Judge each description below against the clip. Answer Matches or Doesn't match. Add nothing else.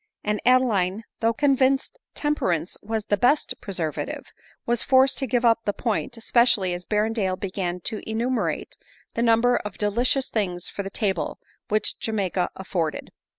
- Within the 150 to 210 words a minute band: Matches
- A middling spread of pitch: Matches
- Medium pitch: Doesn't match